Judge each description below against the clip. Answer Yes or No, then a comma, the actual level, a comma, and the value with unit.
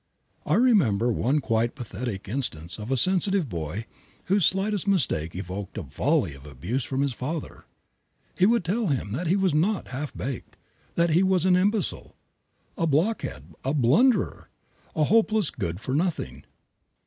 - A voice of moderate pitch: Yes, medium, 145 Hz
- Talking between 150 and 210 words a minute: Yes, average, 160 wpm